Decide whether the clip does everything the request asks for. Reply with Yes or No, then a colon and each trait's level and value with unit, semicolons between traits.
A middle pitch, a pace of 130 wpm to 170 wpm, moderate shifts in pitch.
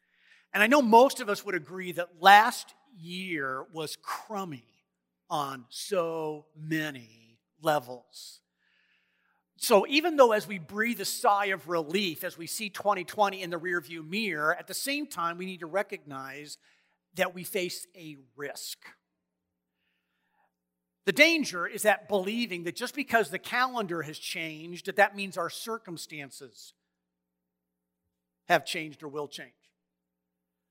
No: medium, 170 Hz; slow, 135 wpm; wide, 7.2 semitones